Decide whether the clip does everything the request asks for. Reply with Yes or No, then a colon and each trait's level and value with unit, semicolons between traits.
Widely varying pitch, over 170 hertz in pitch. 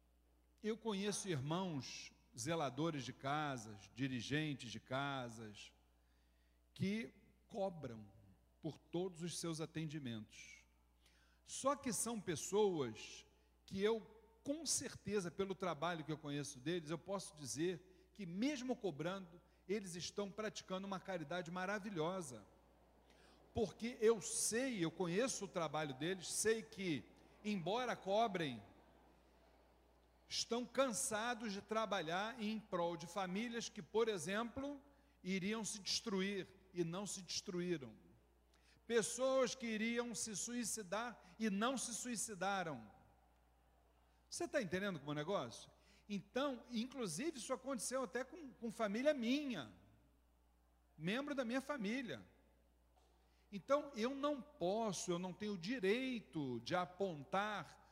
Yes: wide, 8.3 semitones; high, 190 Hz